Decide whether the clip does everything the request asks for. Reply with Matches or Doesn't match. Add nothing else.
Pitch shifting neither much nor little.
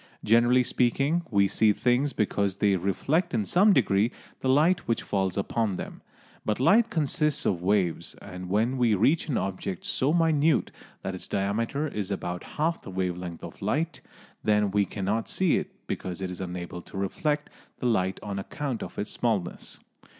Doesn't match